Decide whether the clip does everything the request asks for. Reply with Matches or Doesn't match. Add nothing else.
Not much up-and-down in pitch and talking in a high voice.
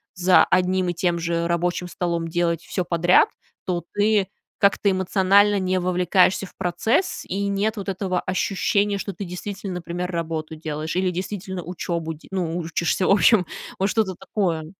Doesn't match